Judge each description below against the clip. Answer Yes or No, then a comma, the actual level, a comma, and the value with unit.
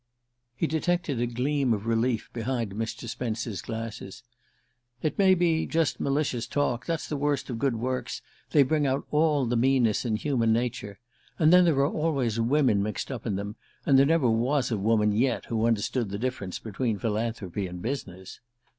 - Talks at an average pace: Yes, average, 180 wpm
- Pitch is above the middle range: No, low, 120 Hz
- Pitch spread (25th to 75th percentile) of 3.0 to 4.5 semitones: Yes, average, 4.1 semitones